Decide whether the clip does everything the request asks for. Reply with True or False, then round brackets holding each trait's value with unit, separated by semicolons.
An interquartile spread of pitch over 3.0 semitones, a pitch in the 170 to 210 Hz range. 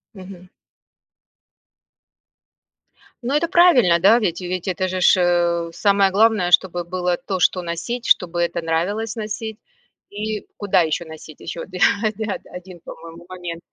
True (3.4 semitones; 185 Hz)